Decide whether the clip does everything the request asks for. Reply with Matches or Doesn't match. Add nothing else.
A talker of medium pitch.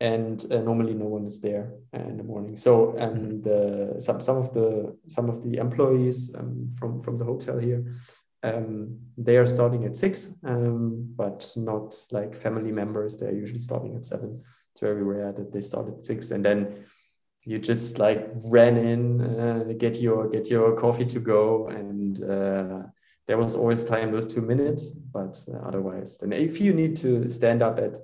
Doesn't match